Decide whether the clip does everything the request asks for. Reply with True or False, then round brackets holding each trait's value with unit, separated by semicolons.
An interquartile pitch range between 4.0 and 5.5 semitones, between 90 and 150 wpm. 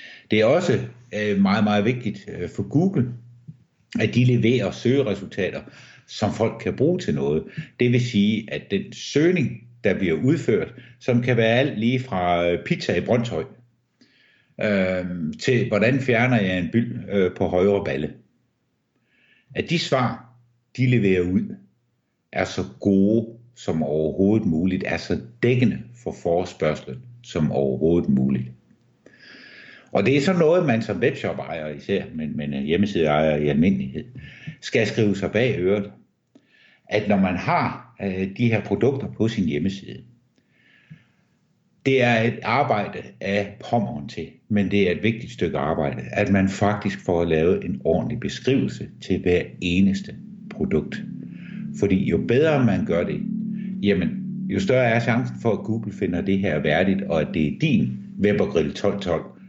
True (4.7 semitones; 145 wpm)